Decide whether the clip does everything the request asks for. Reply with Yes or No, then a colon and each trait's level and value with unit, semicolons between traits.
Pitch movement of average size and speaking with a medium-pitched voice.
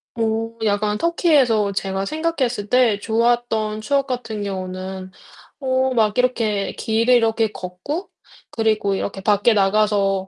No: average, 3.7 semitones; high, 215 Hz